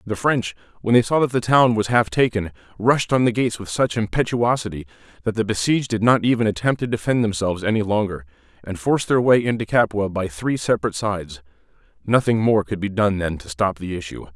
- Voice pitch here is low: Yes, low, 105 Hz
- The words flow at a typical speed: No, fast, 210 wpm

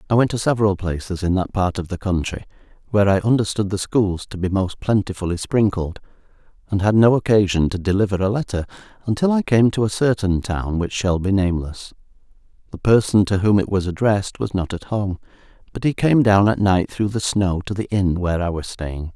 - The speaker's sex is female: No, male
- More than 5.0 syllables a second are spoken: Yes, 5.7 syllables/s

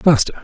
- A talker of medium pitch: Yes, medium, 145 Hz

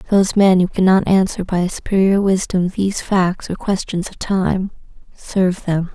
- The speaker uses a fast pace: No, average, 170 wpm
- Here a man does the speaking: No, female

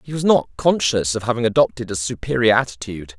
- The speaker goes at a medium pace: Yes, average, 190 wpm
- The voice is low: Yes, low, 115 Hz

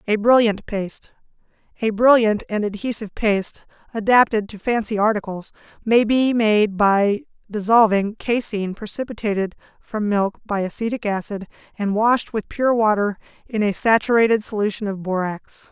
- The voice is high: Yes, high, 215 Hz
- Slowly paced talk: Yes, slow, 130 wpm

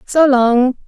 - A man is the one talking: No, female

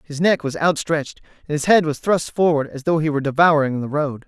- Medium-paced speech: No, fast, 240 wpm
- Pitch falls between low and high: Yes, medium, 155 Hz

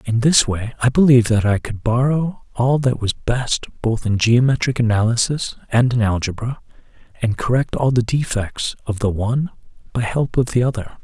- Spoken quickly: No, average, 180 wpm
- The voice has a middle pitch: No, low, 120 Hz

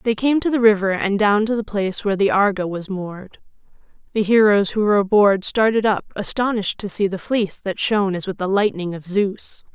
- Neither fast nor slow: No, fast, 215 wpm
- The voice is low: No, high, 205 Hz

